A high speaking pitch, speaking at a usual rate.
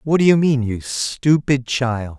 No: low, 130 Hz; average, 190 wpm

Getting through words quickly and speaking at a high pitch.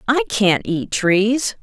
No: average, 150 wpm; high, 205 Hz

